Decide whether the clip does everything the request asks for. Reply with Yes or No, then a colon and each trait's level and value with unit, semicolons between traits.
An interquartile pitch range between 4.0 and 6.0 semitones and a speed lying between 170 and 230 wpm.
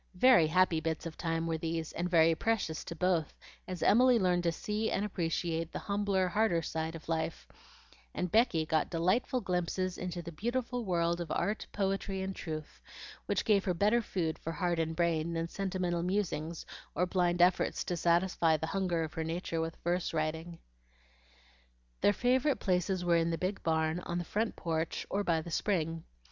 No: average, 2.8 semitones; average, 180 wpm